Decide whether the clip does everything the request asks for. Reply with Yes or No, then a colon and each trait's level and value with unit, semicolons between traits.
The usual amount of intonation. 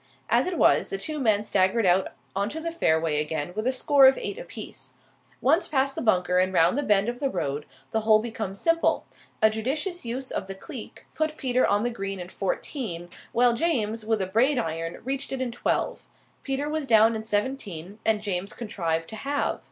No: wide, 5.8 semitones